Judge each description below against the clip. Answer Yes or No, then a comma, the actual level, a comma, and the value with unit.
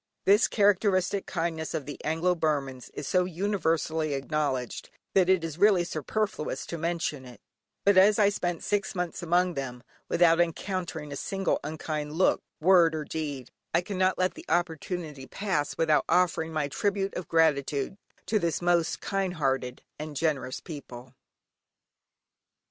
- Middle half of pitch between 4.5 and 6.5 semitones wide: No, average, 3.7 semitones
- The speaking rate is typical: Yes, average, 150 wpm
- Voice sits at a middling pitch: Yes, medium, 165 Hz